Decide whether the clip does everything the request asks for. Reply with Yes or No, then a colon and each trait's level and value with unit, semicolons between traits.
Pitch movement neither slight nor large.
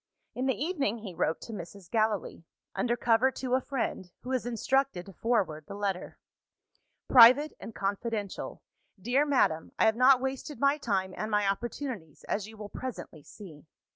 Yes: average, 4.8 semitones